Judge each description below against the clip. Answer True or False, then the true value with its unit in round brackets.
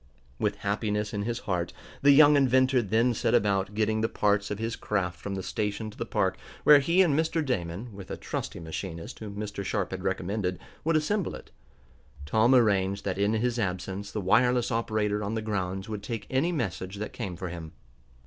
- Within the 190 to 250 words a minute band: True (195 wpm)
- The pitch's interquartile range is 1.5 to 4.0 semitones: True (3.7 semitones)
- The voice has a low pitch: True (105 Hz)